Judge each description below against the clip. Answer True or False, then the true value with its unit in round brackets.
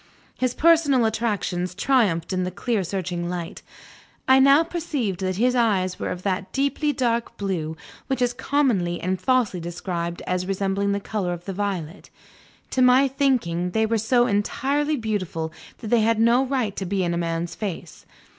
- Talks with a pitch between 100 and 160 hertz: False (205 Hz)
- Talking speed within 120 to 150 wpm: False (175 wpm)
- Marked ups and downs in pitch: True (5.7 semitones)